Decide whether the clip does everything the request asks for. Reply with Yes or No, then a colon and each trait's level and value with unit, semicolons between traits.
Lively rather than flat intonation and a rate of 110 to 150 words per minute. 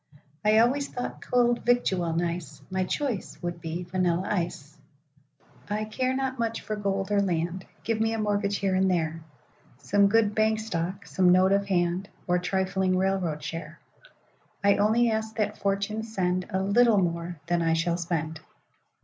No: average, 3.7 semitones; average, 140 wpm